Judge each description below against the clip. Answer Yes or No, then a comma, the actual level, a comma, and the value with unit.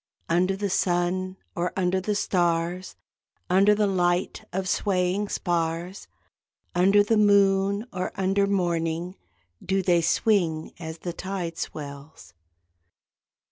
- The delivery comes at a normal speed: No, slow, 115 wpm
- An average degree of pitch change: No, narrow, 2.1 semitones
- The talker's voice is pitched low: No, medium, 185 Hz